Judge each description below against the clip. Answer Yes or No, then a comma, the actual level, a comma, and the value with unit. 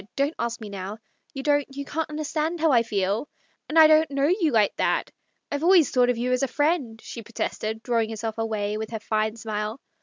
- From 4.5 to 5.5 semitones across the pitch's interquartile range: Yes, average, 5.1 semitones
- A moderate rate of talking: No, fast, 225 wpm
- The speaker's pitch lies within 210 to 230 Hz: No, high, 240 Hz